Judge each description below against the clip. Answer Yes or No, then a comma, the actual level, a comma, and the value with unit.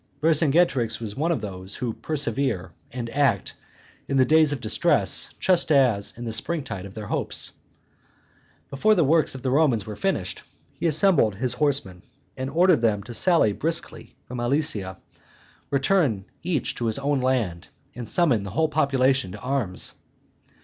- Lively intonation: Yes, wide, 5.9 semitones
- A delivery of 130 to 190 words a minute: Yes, average, 165 wpm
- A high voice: No, low, 130 Hz